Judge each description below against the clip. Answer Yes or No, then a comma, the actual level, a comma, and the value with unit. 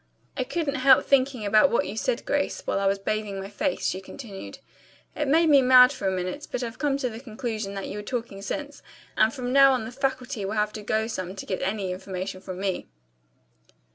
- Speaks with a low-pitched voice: No, high, 220 Hz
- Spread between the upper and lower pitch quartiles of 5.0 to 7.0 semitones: Yes, average, 5.3 semitones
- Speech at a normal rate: No, fast, 225 wpm